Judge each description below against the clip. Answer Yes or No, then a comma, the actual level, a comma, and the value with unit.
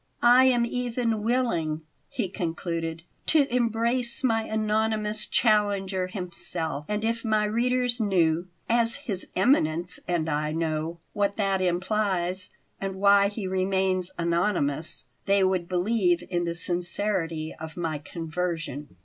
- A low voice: No, high, 190 Hz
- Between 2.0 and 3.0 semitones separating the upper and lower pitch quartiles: No, average, 4.3 semitones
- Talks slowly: Yes, slow, 125 wpm